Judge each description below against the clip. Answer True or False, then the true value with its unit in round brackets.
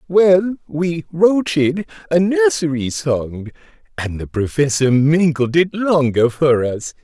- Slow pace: True (120 wpm)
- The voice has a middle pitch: True (150 Hz)